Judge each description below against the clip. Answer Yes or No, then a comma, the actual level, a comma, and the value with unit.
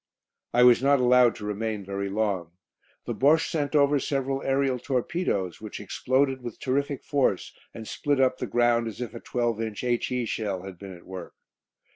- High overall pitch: No, low, 120 Hz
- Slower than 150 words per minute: No, average, 180 wpm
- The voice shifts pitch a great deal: No, average, 4.4 semitones